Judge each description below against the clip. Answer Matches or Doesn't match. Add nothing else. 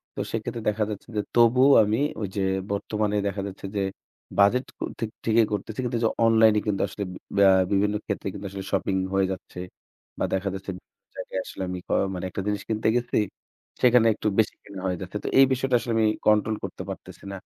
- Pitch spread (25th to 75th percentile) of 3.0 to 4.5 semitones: Doesn't match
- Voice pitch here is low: Matches